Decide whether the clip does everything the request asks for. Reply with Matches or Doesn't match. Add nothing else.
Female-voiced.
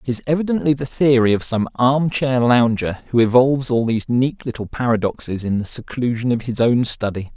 Doesn't match